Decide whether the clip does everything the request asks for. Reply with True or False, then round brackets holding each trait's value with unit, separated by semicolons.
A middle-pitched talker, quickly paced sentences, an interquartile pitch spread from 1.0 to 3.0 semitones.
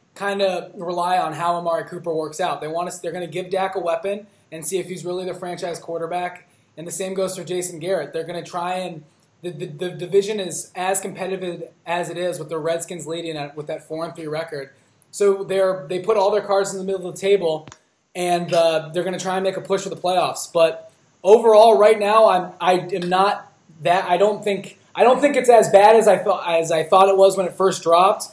True (180 Hz; 245 wpm; 2.4 semitones)